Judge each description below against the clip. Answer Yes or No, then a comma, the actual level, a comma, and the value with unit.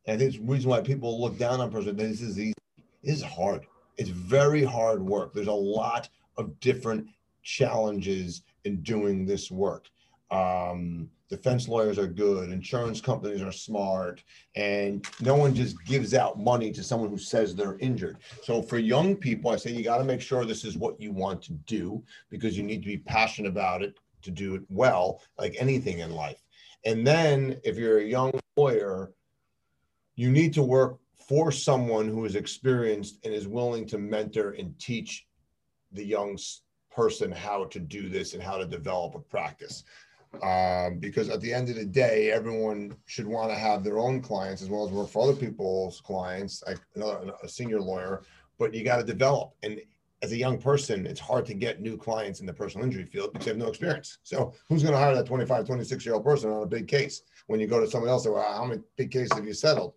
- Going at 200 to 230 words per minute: Yes, fast, 205 wpm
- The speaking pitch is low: Yes, low, 110 Hz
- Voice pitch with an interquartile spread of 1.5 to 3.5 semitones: No, average, 4.1 semitones